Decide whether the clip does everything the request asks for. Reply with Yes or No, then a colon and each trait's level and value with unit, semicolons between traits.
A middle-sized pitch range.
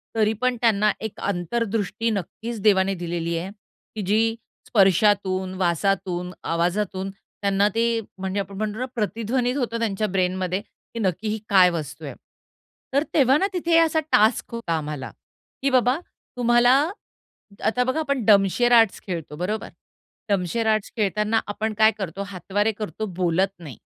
Yes: average, 3.5 semitones